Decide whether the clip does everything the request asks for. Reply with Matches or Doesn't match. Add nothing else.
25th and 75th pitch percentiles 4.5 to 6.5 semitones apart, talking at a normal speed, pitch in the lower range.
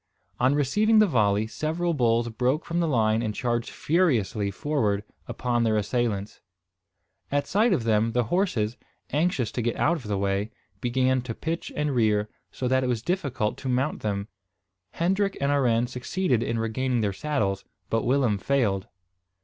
Matches